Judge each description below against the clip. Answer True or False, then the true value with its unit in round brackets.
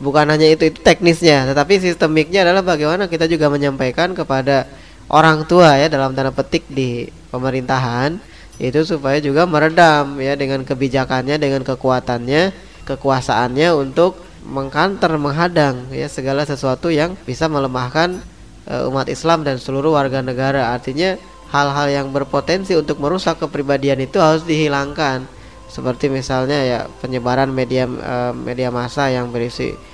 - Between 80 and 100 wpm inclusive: False (135 wpm)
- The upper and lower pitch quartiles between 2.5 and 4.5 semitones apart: True (3.3 semitones)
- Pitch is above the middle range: False (140 Hz)